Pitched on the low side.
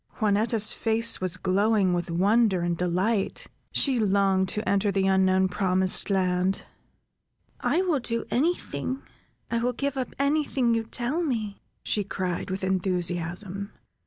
No: high, 200 Hz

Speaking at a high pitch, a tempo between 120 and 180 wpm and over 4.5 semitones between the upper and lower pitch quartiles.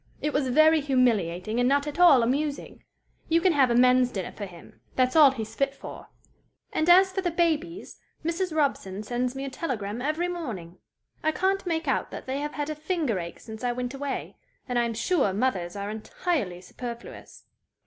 No: very high, 265 Hz; average, 195 wpm; wide, 5.4 semitones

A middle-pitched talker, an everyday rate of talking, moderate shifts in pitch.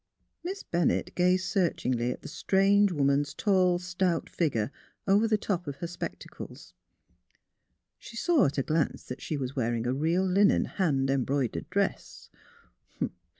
No: medium, 175 Hz; average, 150 wpm; wide, 5.7 semitones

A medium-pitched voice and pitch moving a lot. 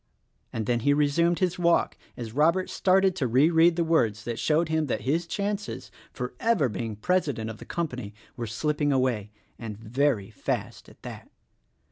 Yes: medium, 145 Hz; wide, 6.6 semitones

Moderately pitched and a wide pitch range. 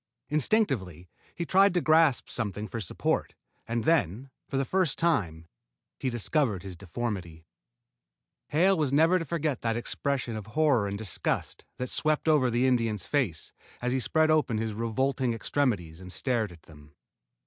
No: low, 120 Hz; wide, 6.8 semitones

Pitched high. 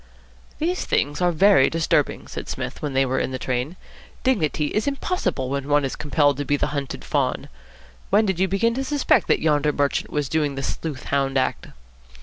No: medium, 150 Hz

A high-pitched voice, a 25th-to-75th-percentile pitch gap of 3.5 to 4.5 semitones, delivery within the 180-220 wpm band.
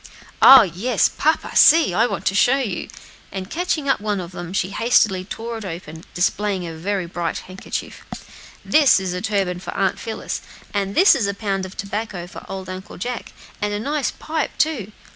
Yes: high, 200 Hz; average, 4.0 semitones; average, 190 wpm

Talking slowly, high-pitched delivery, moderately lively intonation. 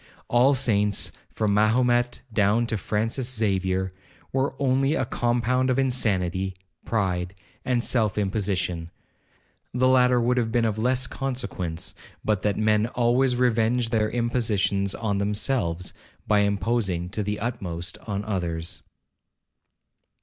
No: slow, 120 wpm; low, 110 Hz; average, 3.8 semitones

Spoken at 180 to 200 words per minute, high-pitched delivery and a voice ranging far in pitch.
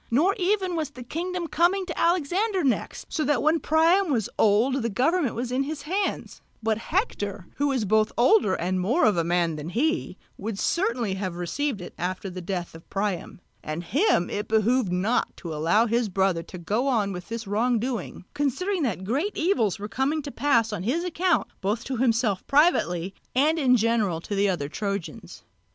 Yes: average, 190 wpm; high, 235 Hz; wide, 7.8 semitones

